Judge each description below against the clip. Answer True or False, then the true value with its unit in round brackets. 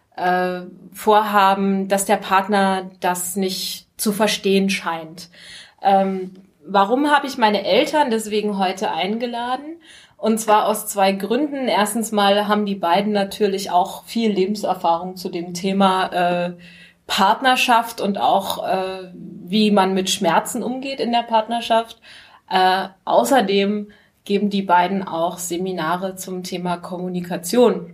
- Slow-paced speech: True (115 wpm)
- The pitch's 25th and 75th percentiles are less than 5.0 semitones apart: True (2.6 semitones)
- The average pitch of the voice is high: True (195 Hz)